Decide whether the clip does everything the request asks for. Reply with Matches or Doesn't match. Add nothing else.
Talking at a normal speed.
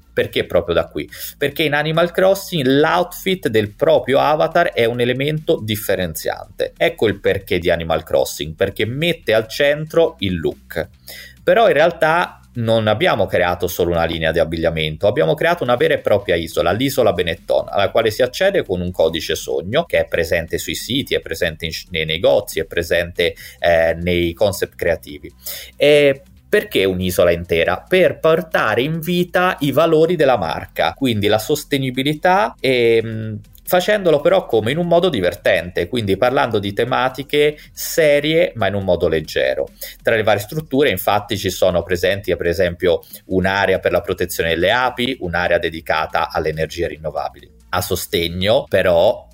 Matches